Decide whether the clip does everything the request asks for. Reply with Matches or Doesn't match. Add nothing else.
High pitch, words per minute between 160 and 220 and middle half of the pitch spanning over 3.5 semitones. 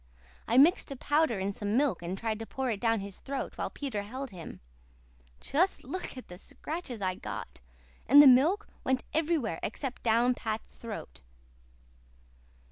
Matches